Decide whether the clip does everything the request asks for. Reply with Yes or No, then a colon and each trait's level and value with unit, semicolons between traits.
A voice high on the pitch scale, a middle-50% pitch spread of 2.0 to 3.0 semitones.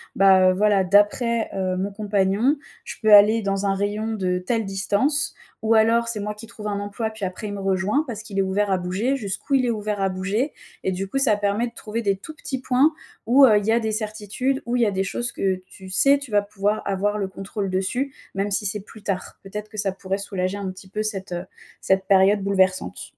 Yes: high, 205 Hz; narrow, 2.5 semitones